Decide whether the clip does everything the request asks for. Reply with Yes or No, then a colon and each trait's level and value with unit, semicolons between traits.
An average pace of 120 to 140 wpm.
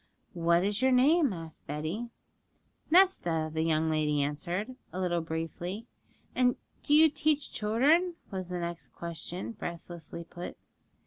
Yes: slow, 135 wpm